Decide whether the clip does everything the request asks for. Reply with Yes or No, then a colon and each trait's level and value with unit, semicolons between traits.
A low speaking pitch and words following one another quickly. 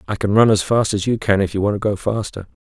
Yes: low, 105 Hz; fast, 320 wpm